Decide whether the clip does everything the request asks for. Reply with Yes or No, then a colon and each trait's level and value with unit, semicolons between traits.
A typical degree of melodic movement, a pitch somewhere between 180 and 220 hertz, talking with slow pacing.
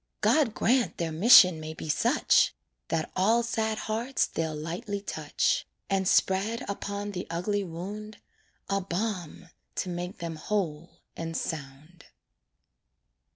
Yes: average, 4.3 semitones; medium, 185 Hz; slow, 125 wpm